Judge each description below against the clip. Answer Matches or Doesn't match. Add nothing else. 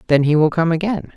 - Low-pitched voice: Doesn't match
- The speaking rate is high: Matches